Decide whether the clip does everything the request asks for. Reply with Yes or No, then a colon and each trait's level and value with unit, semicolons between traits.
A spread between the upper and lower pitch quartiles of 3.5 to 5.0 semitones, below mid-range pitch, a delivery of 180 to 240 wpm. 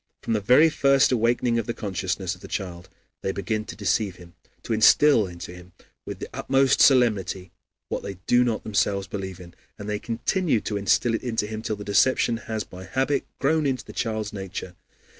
Yes: average, 4.1 semitones; low, 110 Hz; average, 195 wpm